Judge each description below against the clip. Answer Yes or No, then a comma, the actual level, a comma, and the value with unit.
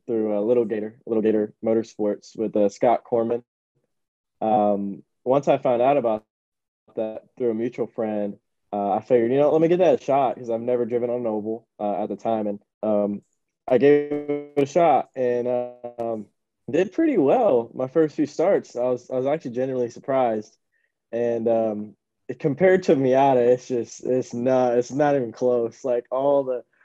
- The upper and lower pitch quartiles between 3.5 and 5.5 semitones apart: No, average, 2.9 semitones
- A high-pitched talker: No, low, 120 Hz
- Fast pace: No, average, 185 wpm